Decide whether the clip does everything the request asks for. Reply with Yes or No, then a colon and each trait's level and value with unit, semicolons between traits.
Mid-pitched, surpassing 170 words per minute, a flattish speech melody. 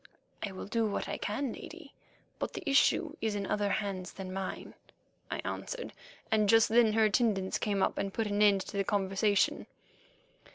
No: high, 205 Hz; average, 180 wpm; narrow, 2.3 semitones